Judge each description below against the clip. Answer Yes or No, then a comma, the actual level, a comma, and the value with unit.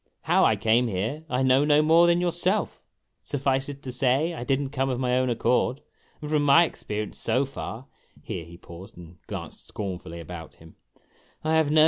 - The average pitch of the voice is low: Yes, low, 130 Hz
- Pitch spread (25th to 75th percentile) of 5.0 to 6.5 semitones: Yes, wide, 5.5 semitones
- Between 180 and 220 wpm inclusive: Yes, average, 200 wpm